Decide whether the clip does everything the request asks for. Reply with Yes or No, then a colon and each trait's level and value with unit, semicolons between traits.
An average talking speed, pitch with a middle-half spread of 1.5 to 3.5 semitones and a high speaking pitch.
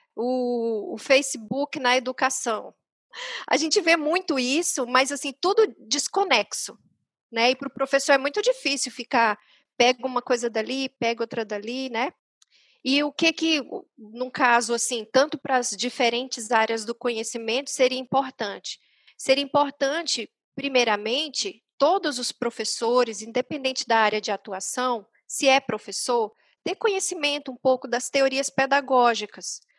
Yes: average, 135 wpm; average, 3.1 semitones; very high, 255 Hz